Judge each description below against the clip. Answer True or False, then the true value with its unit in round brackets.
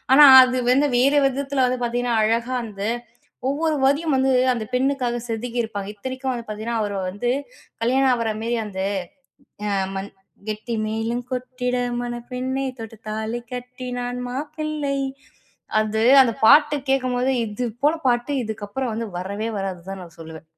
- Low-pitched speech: False (245 Hz)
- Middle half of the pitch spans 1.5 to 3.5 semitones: True (3.2 semitones)